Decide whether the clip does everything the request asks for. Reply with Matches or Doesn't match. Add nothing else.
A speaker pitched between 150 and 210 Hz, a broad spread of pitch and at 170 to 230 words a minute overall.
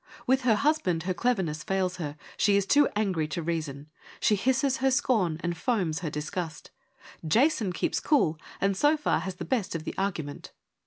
Matches